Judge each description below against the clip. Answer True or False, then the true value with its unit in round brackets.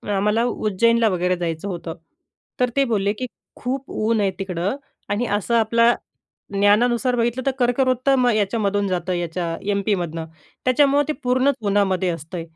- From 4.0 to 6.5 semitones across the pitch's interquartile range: True (4.7 semitones)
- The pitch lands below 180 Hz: False (210 Hz)